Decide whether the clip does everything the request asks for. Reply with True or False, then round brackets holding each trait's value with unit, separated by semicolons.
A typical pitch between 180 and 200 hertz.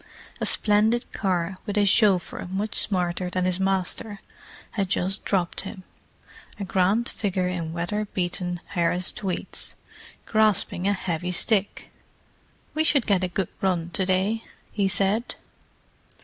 True (190 Hz)